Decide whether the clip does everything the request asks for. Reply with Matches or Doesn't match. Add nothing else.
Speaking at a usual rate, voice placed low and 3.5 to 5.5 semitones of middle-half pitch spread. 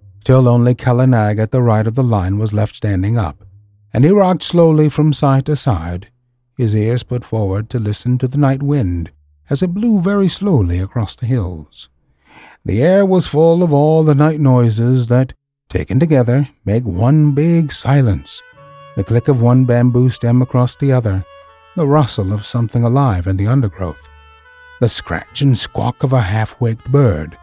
Matches